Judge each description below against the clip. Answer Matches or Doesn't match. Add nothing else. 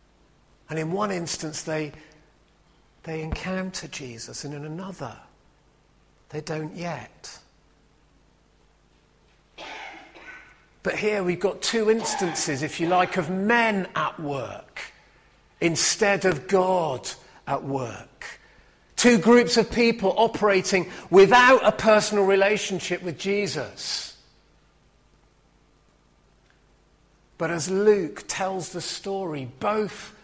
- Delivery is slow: Matches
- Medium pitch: Matches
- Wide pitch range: Doesn't match